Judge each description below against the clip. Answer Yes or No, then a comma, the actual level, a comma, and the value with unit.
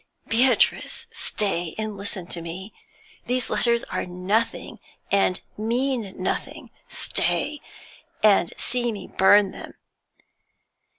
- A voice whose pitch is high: Yes, high, 210 Hz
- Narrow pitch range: No, average, 3.9 semitones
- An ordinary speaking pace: No, slow, 105 wpm